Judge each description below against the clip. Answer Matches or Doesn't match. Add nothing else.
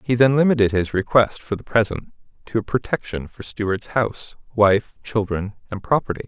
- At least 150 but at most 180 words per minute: Matches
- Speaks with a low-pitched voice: Matches